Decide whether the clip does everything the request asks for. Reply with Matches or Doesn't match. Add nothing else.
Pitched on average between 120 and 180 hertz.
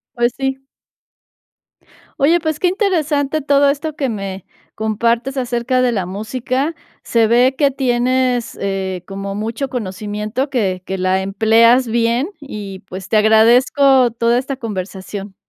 Doesn't match